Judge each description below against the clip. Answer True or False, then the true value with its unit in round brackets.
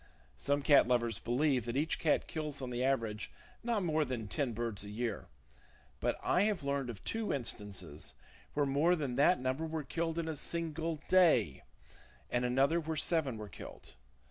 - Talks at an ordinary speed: True (175 wpm)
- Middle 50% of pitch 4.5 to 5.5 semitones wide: True (5.2 semitones)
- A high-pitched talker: False (140 Hz)